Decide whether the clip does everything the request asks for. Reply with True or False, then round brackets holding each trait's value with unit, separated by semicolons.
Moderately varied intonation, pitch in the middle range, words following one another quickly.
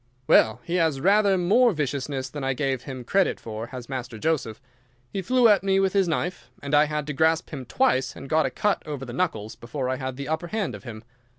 False (5.8 semitones; 145 Hz; 230 wpm)